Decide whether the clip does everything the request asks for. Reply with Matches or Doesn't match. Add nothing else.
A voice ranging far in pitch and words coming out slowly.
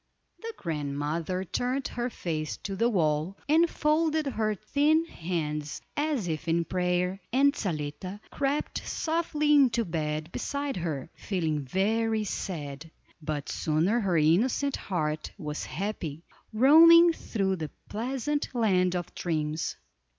Matches